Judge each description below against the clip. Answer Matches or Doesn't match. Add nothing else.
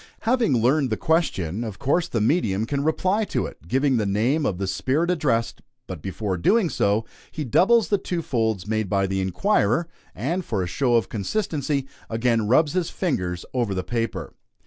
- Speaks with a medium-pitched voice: Doesn't match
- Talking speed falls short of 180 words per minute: Doesn't match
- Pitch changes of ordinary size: Doesn't match